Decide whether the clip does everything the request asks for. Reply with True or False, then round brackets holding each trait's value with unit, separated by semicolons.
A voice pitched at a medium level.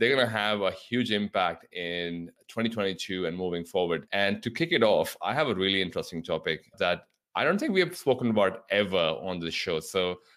False (100 Hz)